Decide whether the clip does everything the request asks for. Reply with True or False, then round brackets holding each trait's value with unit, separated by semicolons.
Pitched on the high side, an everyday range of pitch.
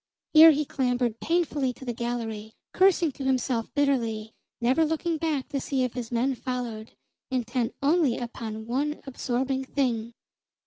True (255 Hz; 3.4 semitones)